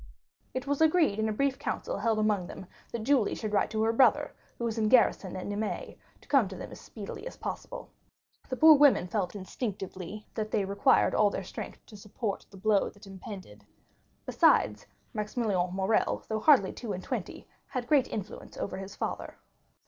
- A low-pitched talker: No, high, 215 Hz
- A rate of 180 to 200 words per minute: Yes, average, 185 wpm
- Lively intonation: No, average, 3.6 semitones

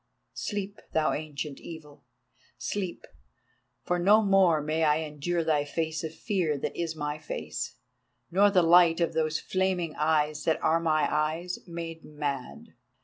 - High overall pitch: No, medium, 160 Hz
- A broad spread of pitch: No, narrow, 2.5 semitones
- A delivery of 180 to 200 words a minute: No, average, 145 wpm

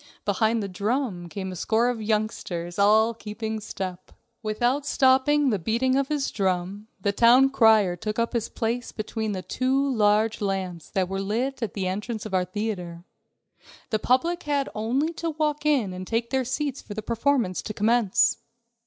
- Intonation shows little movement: No, average, 4.6 semitones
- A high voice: Yes, high, 220 Hz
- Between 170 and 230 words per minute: Yes, average, 175 wpm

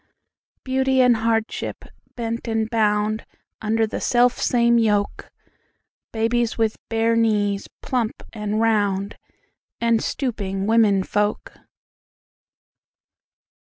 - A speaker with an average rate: No, slow, 80 wpm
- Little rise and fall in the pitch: Yes, narrow, 1.9 semitones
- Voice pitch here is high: Yes, high, 225 Hz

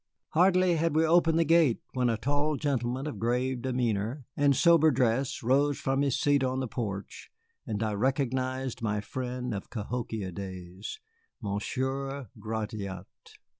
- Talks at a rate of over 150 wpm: No, average, 145 wpm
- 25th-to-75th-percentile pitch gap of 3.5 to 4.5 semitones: Yes, average, 4.2 semitones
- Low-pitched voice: Yes, low, 130 Hz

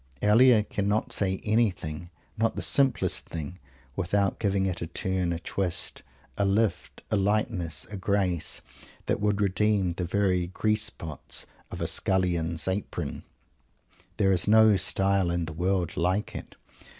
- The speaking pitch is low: Yes, very low, 95 Hz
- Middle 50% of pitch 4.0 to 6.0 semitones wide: No, average, 3.0 semitones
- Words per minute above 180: No, average, 145 wpm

